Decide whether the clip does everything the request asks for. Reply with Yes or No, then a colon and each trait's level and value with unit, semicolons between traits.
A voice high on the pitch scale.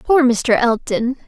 Yes: very high, 250 Hz